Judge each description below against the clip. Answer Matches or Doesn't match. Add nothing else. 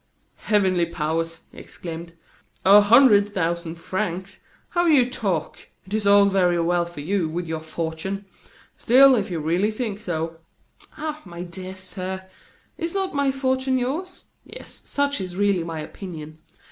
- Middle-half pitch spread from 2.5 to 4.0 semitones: Doesn't match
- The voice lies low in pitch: Doesn't match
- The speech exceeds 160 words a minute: Doesn't match